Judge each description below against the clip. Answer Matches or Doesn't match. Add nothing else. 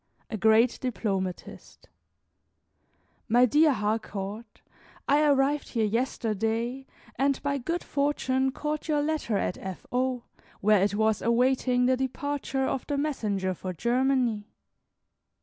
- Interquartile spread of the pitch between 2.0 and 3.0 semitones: Doesn't match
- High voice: Matches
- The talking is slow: Matches